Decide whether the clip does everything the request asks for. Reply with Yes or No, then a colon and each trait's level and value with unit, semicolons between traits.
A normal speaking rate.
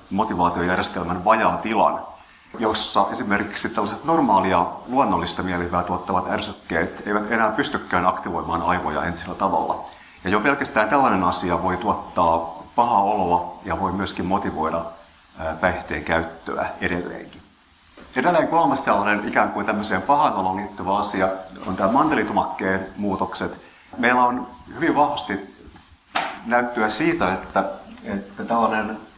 Yes: average, 115 wpm